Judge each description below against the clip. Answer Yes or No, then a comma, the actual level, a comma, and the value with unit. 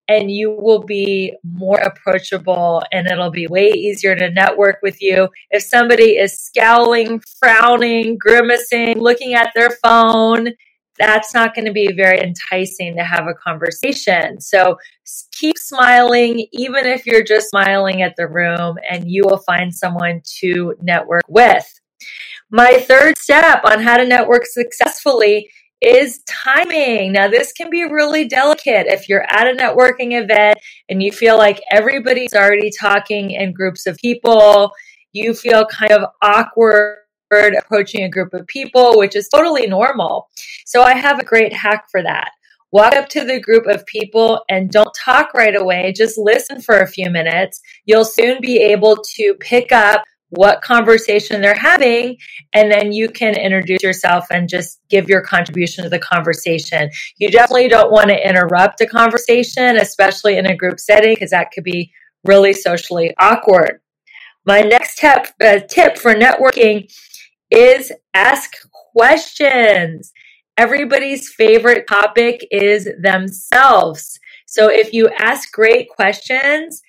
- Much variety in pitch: No, average, 3.9 semitones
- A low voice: No, high, 215 Hz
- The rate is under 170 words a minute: Yes, average, 150 wpm